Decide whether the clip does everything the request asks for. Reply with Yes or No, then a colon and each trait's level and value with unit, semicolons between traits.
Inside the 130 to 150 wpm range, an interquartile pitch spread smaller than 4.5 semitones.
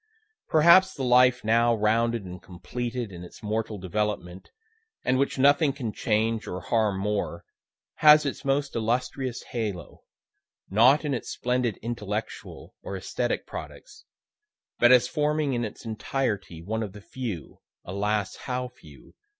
Yes: average, 140 wpm; average, 3.6 semitones